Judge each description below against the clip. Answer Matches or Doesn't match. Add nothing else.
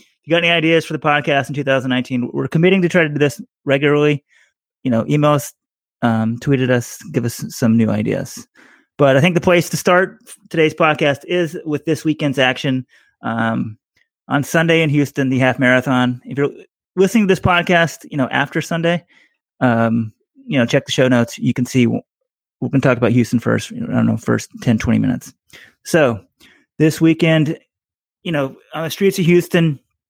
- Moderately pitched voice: Matches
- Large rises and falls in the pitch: Doesn't match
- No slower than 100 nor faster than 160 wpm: Doesn't match